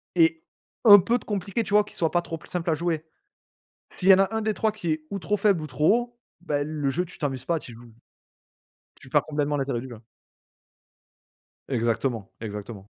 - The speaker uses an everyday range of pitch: No, wide, 6.9 semitones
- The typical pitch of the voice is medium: Yes, medium, 165 Hz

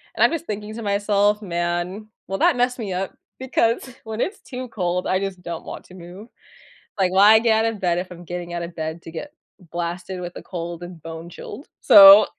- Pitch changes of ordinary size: Yes, average, 3.8 semitones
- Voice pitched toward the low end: No, high, 190 Hz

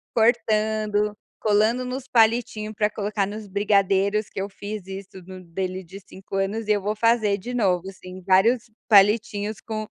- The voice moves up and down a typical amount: No, narrow, 2.0 semitones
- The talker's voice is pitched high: Yes, high, 210 Hz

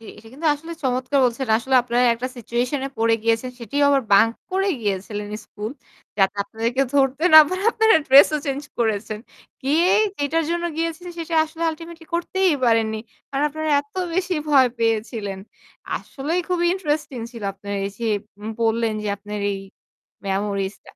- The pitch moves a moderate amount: No, wide, 6.1 semitones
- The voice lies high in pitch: Yes, very high, 255 Hz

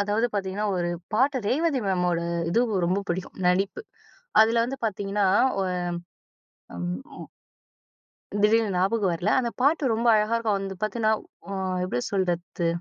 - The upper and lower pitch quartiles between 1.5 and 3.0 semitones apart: No, average, 3.8 semitones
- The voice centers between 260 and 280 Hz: No, high, 205 Hz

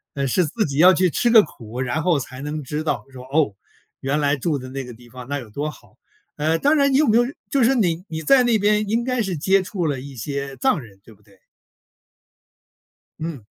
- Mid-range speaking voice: Yes, medium, 150 Hz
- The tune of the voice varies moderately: No, wide, 7.1 semitones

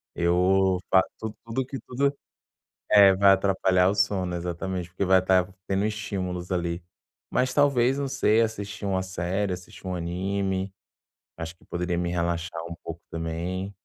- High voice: No, very low, 95 Hz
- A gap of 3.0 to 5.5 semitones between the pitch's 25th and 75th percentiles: No, narrow, 2.5 semitones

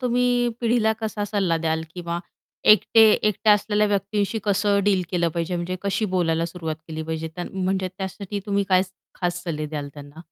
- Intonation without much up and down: No, average, 3.8 semitones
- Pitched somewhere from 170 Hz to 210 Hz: Yes, high, 190 Hz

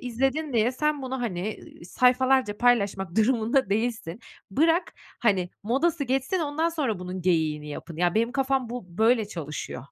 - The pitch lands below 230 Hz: No, high, 235 Hz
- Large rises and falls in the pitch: Yes, wide, 5.7 semitones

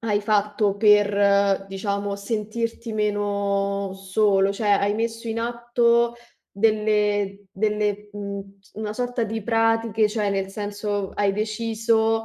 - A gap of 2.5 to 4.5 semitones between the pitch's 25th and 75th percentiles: No, narrow, 1.9 semitones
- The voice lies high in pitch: Yes, high, 210 Hz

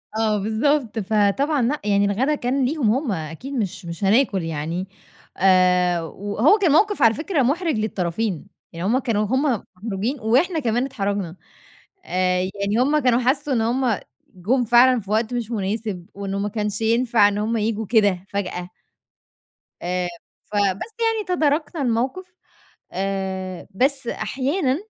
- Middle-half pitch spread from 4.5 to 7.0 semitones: Yes, average, 5.2 semitones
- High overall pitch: Yes, high, 220 Hz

